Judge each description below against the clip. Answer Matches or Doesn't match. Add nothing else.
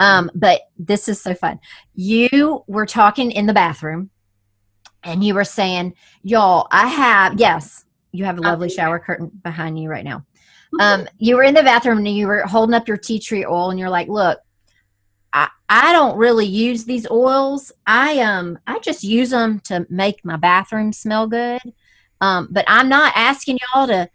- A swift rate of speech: Doesn't match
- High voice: Matches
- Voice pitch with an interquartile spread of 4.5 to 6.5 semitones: Matches